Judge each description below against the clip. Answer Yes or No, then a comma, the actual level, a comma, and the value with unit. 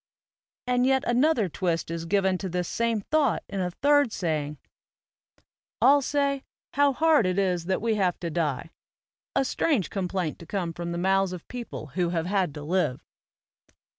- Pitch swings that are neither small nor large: No, wide, 6.4 semitones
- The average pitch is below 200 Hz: Yes, high, 190 Hz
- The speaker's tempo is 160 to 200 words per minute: Yes, average, 170 wpm